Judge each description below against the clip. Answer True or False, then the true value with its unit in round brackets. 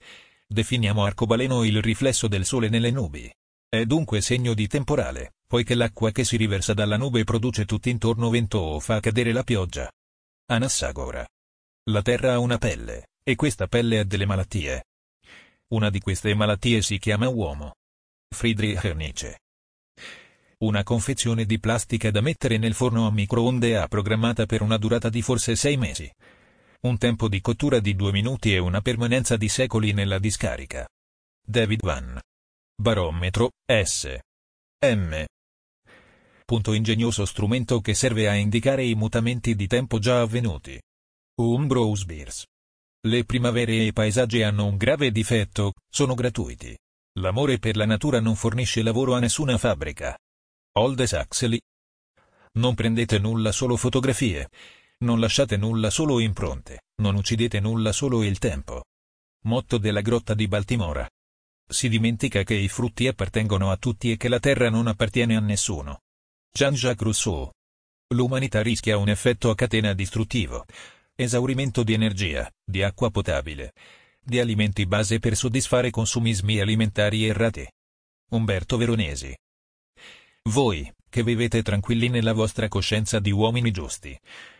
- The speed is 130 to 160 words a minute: True (140 wpm)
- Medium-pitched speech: False (110 Hz)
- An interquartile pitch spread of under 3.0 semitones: False (3.4 semitones)